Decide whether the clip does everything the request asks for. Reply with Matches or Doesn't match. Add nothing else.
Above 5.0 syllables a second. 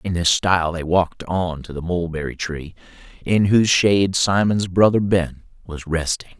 Doesn't match